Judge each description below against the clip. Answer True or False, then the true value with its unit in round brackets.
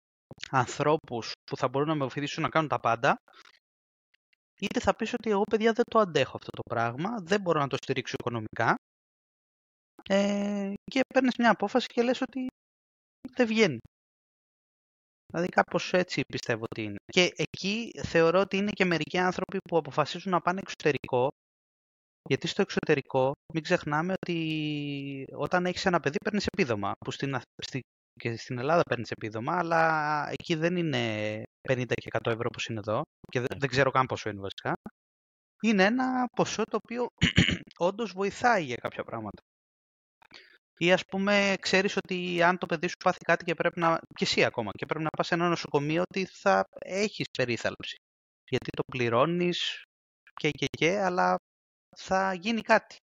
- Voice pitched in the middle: True (165 Hz)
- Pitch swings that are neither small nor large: False (6.9 semitones)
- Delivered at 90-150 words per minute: False (165 wpm)